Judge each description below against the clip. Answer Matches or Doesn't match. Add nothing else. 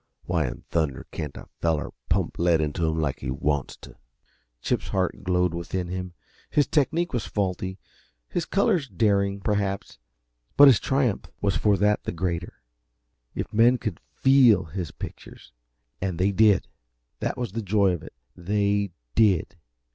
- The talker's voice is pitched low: Matches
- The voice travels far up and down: Doesn't match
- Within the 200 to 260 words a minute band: Doesn't match